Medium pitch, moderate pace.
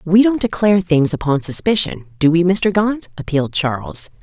Yes: medium, 170 Hz; average, 170 wpm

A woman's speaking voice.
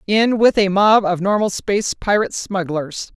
Yes: female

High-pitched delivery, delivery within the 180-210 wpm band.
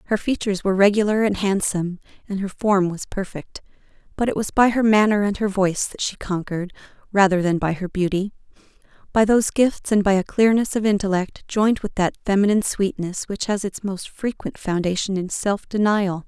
Yes: high, 200 Hz; average, 185 wpm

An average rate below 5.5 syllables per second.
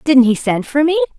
No: 5.6 syllables/s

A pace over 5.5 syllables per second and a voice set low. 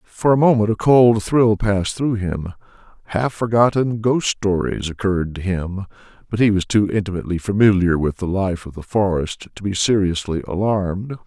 No: 5.0 syllables/s; low, 100 Hz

